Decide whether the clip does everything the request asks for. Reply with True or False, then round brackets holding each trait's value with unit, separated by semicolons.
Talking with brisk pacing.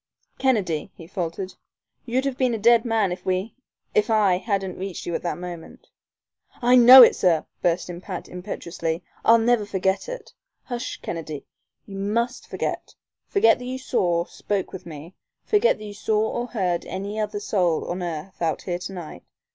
False (180 wpm)